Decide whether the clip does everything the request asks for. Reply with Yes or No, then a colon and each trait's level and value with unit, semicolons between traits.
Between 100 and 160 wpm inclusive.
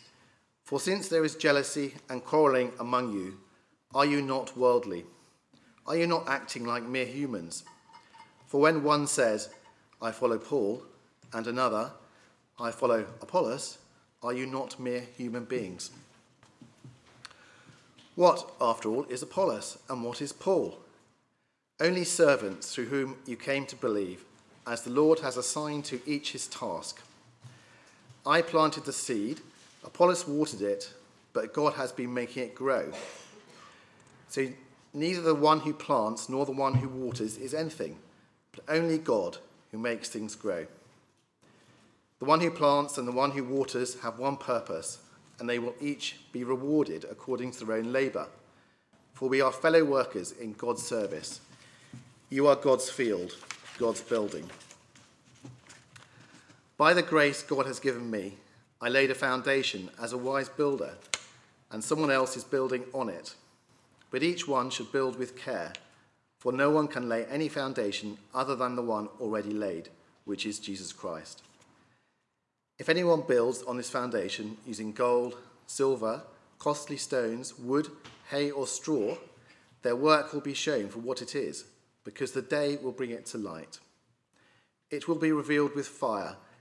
Yes: average, 150 wpm